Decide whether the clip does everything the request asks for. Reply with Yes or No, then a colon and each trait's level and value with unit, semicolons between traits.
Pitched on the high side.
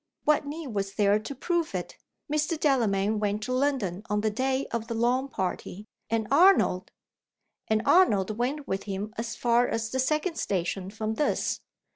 Yes: high, 230 Hz